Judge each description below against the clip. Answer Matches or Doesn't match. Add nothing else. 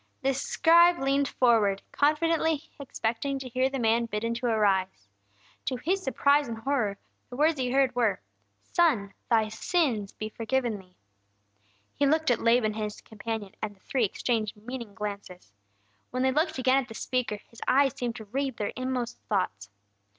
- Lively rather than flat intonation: Doesn't match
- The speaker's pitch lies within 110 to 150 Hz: Doesn't match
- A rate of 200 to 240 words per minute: Doesn't match